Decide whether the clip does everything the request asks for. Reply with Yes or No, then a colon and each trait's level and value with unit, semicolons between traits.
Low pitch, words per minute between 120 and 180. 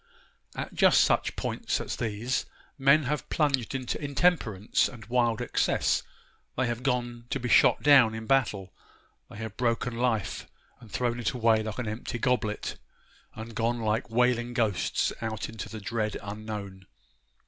Yes: low, 115 Hz; average, 155 wpm